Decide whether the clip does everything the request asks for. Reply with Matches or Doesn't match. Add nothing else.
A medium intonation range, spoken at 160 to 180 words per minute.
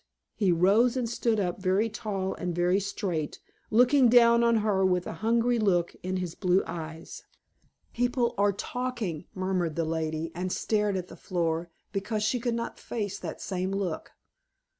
Matches